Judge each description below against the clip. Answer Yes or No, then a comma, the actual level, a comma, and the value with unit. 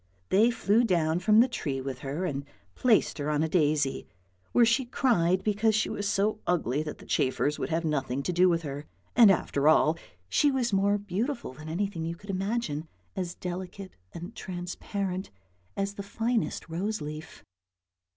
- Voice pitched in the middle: Yes, medium, 180 Hz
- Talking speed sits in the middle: Yes, average, 175 wpm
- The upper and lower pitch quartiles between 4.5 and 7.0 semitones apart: Yes, average, 5.2 semitones